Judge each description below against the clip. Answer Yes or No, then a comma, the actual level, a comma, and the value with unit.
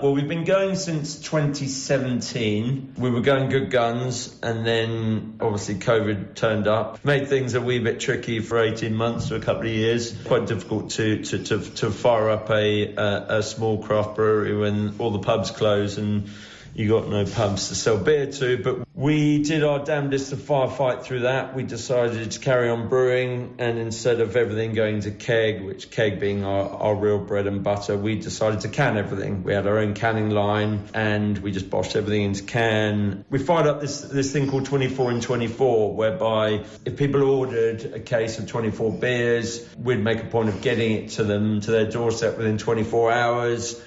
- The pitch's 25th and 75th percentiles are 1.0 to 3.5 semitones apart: Yes, average, 3.2 semitones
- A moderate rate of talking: Yes, average, 195 wpm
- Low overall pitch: Yes, low, 115 Hz